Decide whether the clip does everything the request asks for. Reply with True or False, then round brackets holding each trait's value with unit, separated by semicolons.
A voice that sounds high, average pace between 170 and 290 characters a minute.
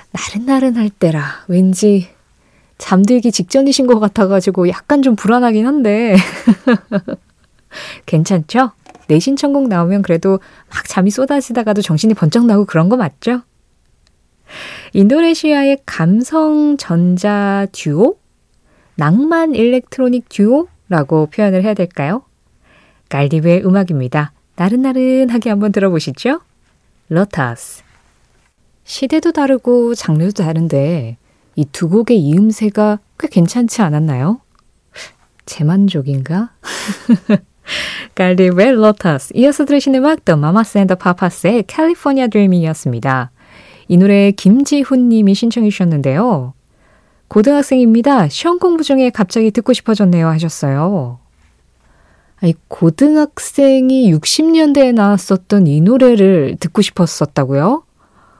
True (205 Hz; 265 characters per minute)